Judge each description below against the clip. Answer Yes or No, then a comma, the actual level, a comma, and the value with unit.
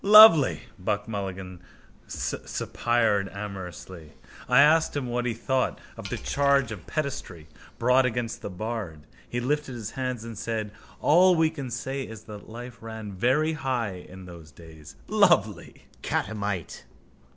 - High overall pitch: No, low, 115 Hz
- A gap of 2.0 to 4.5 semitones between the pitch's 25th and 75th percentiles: No, average, 5.2 semitones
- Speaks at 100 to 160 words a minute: Yes, average, 140 wpm